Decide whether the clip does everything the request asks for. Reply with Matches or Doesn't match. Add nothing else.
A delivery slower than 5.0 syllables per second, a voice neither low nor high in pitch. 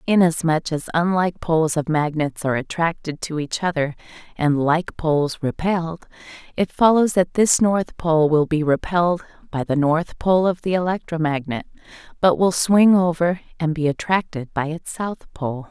Matches